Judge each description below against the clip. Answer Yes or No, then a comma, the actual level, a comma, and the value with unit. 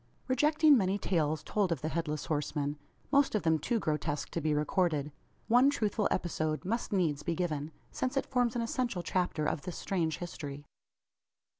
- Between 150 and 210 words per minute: Yes, average, 170 wpm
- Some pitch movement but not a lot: No, wide, 6.9 semitones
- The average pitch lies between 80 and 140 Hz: No, medium, 175 Hz